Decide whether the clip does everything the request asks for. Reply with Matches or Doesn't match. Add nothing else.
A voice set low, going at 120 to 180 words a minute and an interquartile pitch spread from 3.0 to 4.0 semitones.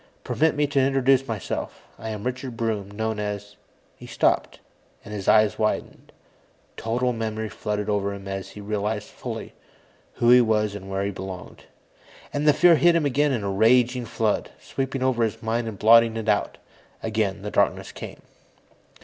Matches